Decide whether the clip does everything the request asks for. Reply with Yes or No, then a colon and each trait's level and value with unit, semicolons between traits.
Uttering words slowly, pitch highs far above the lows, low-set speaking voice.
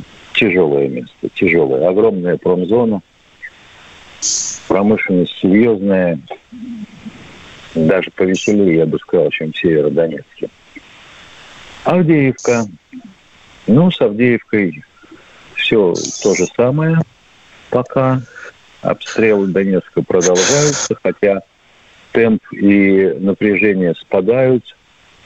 Yes: slow, 75 wpm; wide, 6.3 semitones; low, 110 Hz